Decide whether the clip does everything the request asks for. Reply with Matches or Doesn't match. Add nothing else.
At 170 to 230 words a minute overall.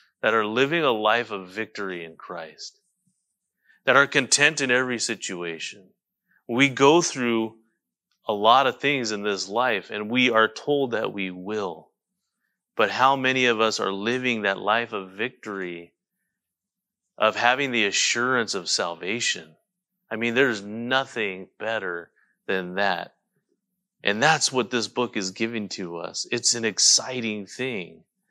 Doesn't match